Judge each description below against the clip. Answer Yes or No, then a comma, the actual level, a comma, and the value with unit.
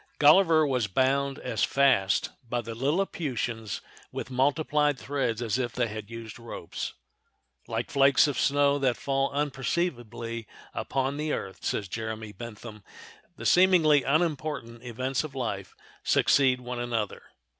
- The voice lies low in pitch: Yes, low, 130 Hz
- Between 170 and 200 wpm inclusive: No, slow, 135 wpm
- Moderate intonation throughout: Yes, average, 3.7 semitones